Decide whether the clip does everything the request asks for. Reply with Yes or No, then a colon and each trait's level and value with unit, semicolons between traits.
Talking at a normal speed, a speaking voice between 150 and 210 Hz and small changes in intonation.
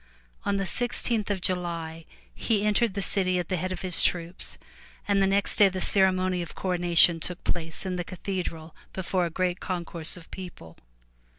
Yes: average, 180 wpm; medium, 185 Hz; narrow, 2.1 semitones